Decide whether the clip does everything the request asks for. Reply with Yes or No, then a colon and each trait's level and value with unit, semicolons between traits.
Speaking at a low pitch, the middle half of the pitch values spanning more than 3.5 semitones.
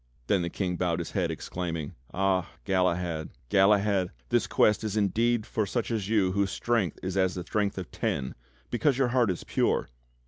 No: very low, 95 Hz; average, 3.1 semitones